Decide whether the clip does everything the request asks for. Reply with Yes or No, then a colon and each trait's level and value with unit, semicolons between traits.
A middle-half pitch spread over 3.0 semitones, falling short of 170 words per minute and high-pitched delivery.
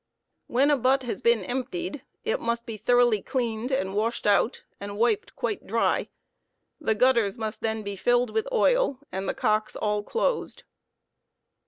Yes: average, 3.8 semitones; average, 160 wpm; high, 235 Hz